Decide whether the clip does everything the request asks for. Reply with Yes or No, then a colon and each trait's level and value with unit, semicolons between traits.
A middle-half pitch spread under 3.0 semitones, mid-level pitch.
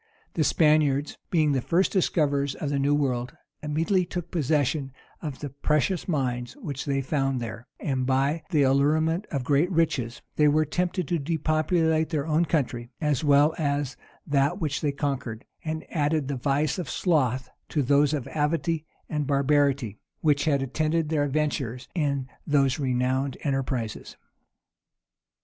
Yes: narrow, 2.5 semitones; medium, 145 Hz